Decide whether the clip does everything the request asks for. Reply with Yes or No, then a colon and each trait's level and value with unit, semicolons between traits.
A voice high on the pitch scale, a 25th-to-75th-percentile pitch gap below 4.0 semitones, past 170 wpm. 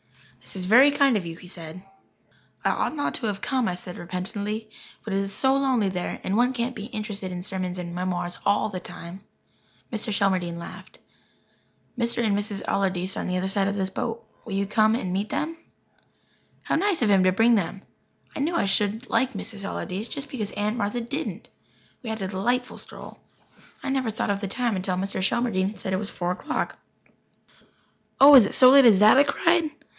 No: high, 205 Hz; average, 4.3 semitones; fast, 205 wpm